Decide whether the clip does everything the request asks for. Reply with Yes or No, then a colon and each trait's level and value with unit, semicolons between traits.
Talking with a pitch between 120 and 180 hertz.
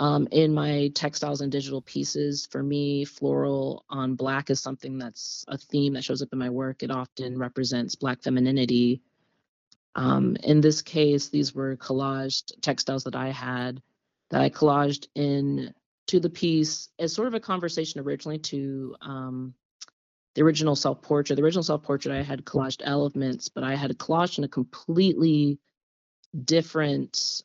Yes: medium, 140 Hz